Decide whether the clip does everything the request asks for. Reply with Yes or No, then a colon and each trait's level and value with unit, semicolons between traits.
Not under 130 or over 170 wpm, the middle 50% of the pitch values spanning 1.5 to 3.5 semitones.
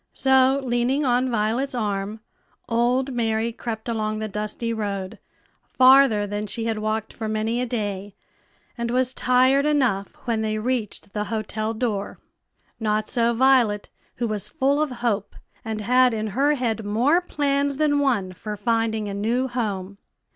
Yes: average, 155 wpm; average, 3.2 semitones